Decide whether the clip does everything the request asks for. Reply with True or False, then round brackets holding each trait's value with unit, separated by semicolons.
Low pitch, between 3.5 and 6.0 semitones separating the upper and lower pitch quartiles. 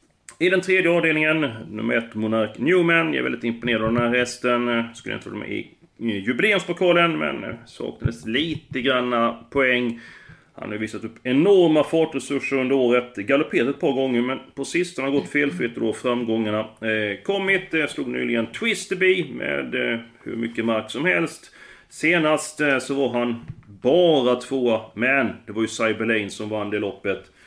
True (125 Hz; 5.2 semitones)